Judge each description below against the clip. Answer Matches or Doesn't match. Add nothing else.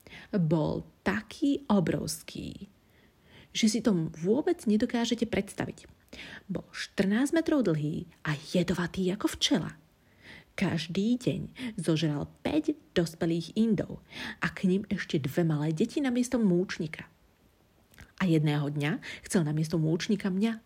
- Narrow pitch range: Doesn't match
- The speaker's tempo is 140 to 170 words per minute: Doesn't match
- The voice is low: Doesn't match